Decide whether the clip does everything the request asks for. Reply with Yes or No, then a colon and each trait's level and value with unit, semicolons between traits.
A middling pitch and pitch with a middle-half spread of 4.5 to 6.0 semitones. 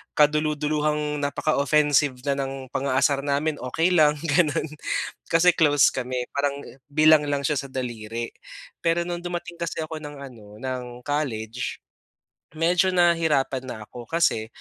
No: medium, 145 Hz; average, 3.2 semitones